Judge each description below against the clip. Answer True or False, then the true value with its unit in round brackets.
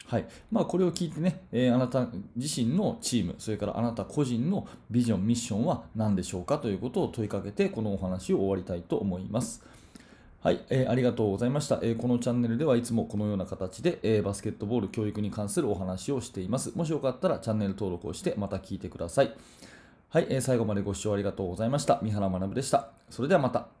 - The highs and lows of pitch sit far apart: False (4.2 semitones)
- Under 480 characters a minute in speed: False (495 characters per minute)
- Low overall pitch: True (115 Hz)